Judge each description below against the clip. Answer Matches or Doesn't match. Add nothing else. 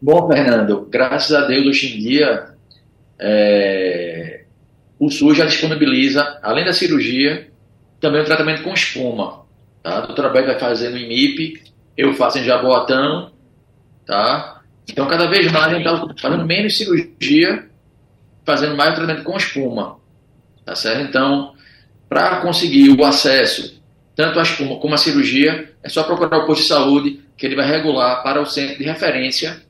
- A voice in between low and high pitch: Matches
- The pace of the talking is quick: Doesn't match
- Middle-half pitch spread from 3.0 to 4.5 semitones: Matches